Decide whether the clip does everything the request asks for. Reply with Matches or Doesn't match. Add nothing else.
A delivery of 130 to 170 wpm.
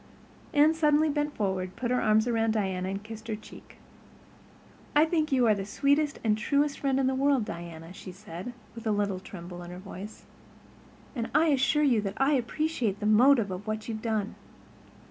Doesn't match